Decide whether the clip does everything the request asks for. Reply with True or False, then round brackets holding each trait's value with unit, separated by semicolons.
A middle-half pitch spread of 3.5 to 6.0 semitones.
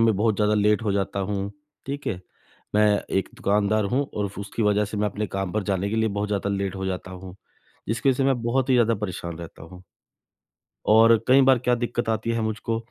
False (2.7 semitones)